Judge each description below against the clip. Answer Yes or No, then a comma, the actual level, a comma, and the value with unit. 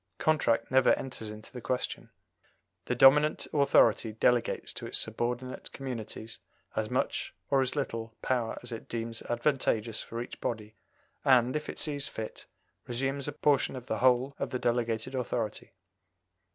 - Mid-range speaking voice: No, low, 125 Hz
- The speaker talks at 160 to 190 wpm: No, average, 150 wpm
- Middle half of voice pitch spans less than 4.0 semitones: Yes, average, 2.8 semitones